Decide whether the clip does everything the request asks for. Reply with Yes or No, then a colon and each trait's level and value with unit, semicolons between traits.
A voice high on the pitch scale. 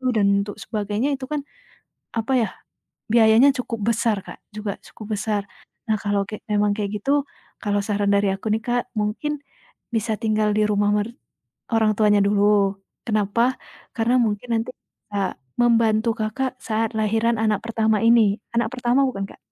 Yes: high, 215 Hz